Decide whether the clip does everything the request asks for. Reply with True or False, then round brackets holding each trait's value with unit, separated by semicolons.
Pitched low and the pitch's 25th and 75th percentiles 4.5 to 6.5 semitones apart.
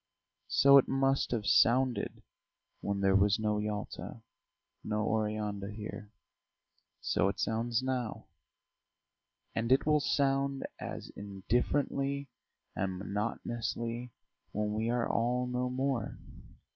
False (115 Hz; 3.8 semitones)